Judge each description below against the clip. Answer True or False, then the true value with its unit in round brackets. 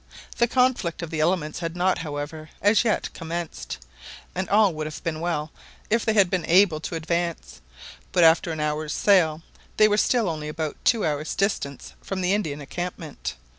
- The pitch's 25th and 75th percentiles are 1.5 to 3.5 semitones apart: False (4.0 semitones)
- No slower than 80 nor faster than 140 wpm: False (180 wpm)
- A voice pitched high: False (170 Hz)